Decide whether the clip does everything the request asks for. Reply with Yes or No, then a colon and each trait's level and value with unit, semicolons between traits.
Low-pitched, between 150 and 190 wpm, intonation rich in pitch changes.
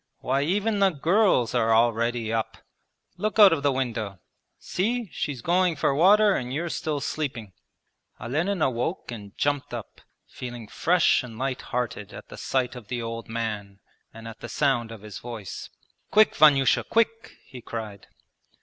Yes: low, 125 Hz; average, 160 wpm; wide, 6.7 semitones